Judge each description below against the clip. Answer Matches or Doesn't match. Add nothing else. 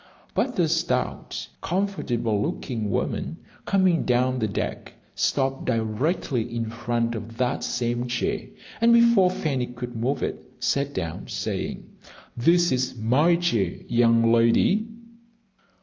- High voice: Doesn't match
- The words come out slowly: Matches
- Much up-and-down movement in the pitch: Matches